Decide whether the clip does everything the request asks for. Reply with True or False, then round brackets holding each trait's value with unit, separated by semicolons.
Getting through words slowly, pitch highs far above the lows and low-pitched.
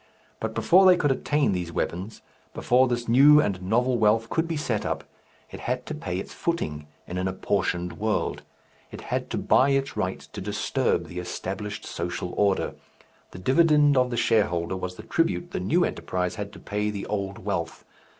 False (185 wpm; 6.8 semitones; 105 Hz)